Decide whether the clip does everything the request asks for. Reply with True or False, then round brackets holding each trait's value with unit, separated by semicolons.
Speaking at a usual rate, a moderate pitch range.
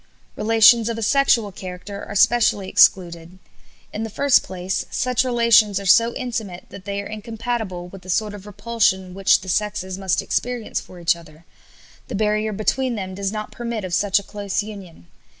True (180 wpm; 3.3 semitones)